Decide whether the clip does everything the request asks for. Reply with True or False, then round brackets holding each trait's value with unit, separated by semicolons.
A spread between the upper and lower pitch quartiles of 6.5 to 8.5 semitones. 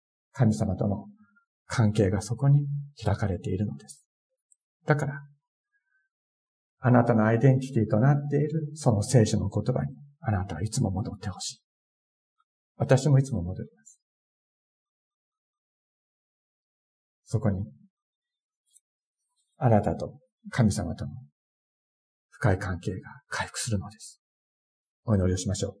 True (7.1 semitones)